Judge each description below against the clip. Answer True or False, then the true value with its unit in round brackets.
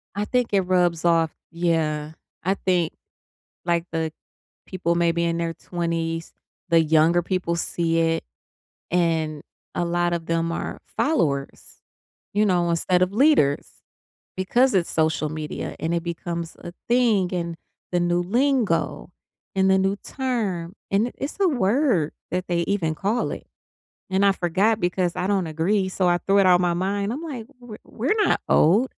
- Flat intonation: False (3.1 semitones)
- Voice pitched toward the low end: False (175 Hz)